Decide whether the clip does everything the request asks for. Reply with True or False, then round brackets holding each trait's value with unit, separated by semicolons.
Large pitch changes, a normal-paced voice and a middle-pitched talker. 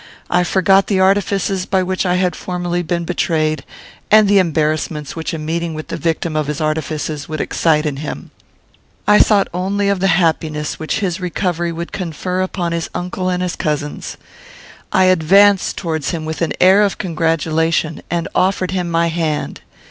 False (2.9 semitones; 175 wpm; 170 Hz)